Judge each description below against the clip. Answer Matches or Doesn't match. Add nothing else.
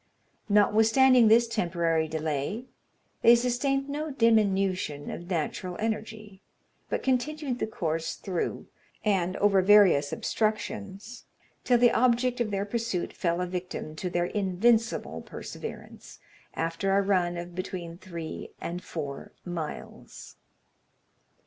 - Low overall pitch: Doesn't match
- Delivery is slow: Matches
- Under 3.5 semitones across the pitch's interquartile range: Doesn't match